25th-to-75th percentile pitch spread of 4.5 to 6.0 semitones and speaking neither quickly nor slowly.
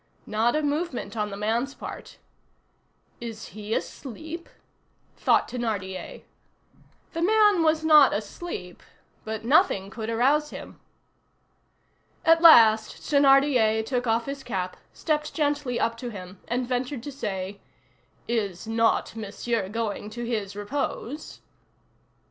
No: average, 5.2 semitones; slow, 120 wpm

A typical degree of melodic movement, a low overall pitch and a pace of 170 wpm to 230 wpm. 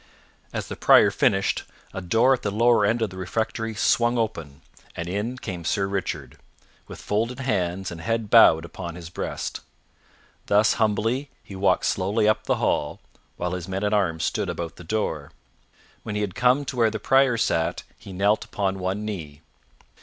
Yes: average, 3.9 semitones; low, 100 Hz; average, 180 wpm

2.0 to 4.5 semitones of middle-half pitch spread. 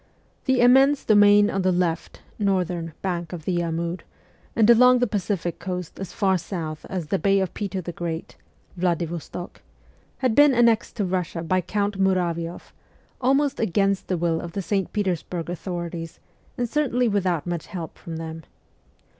Yes: average, 3.3 semitones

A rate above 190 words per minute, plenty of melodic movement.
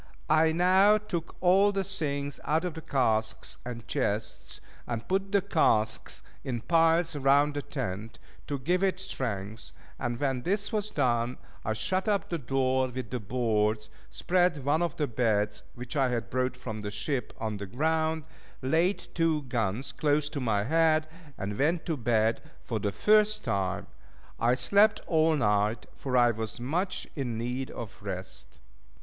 No: average, 165 wpm; wide, 6.5 semitones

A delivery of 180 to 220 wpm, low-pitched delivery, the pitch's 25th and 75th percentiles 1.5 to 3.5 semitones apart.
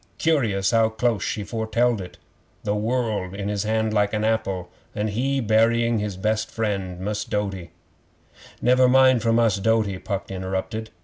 No: average, 165 wpm; low, 110 Hz; narrow, 2.4 semitones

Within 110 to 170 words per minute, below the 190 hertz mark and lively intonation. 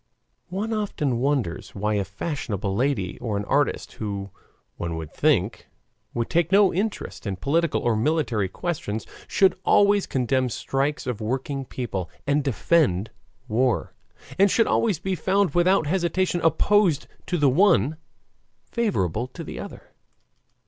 Yes: average, 140 wpm; medium, 140 Hz; wide, 8.5 semitones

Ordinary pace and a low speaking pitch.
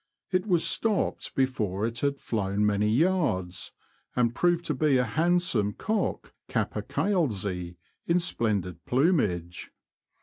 No: slow, 115 wpm; low, 125 Hz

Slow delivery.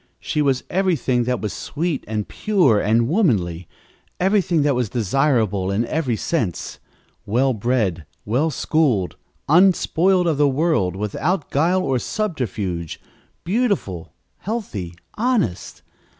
Yes: slow, 120 wpm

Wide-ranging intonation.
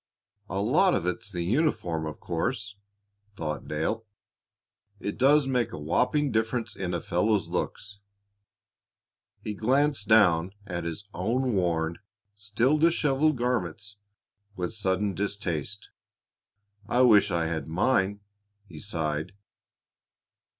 Yes: wide, 6.0 semitones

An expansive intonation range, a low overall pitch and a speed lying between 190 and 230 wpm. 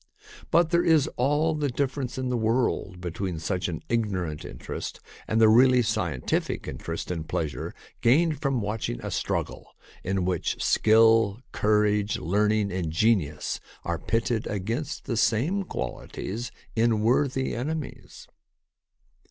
No: wide, 5.7 semitones; low, 110 Hz; slow, 135 wpm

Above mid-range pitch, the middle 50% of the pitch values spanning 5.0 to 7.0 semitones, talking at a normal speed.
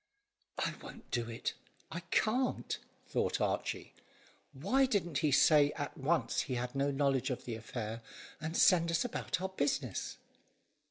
No: medium, 145 Hz; average, 5.3 semitones; average, 155 wpm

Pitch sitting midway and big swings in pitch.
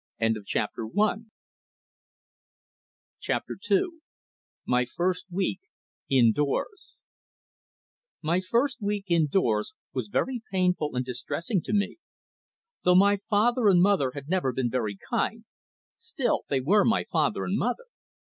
Yes: medium, 180 Hz; wide, 7.5 semitones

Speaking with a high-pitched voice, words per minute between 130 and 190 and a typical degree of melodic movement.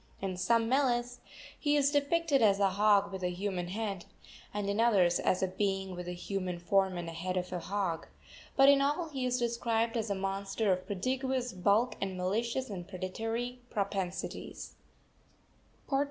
Yes: high, 200 Hz; average, 170 wpm; average, 4.5 semitones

